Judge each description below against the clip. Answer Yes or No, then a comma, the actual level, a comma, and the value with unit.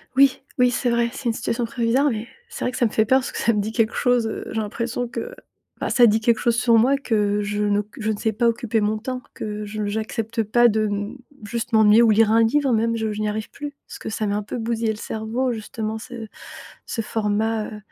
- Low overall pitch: No, high, 225 Hz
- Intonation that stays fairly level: Yes, narrow, 1.9 semitones